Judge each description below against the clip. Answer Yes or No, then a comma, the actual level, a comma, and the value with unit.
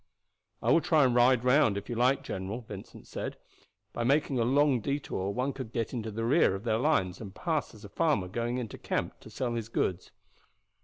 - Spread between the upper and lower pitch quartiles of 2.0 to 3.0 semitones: No, average, 4.1 semitones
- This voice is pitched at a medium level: No, low, 120 Hz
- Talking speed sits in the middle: No, fast, 210 wpm